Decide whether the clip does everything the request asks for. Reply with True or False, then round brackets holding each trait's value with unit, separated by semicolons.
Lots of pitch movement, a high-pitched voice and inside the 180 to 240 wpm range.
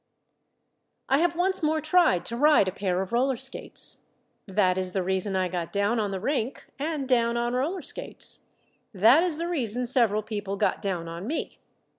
True (7.4 semitones; 230 Hz; 185 wpm)